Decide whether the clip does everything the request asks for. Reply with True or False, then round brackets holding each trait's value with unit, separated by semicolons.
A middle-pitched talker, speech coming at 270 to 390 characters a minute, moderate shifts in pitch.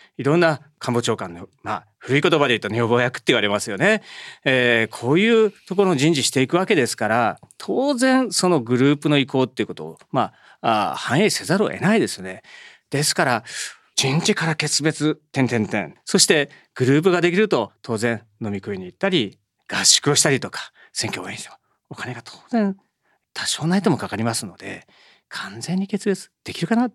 False (145 Hz; 360 characters per minute; 7.9 semitones)